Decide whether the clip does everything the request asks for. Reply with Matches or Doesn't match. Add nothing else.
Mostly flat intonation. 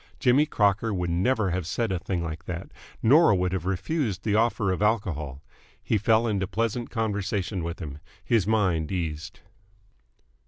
Doesn't match